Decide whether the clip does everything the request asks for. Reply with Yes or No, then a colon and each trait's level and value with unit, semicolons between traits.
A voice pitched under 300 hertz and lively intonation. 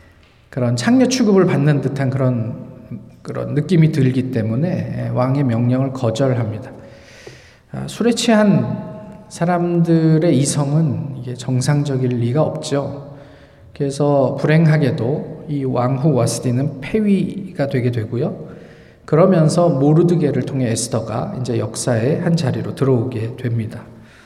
No: medium, 140 Hz; average, 4.6 semitones